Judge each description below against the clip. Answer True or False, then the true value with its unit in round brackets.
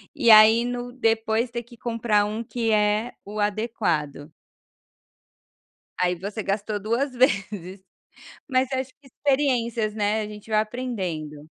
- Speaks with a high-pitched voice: True (220 Hz)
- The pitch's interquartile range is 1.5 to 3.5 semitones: True (2.7 semitones)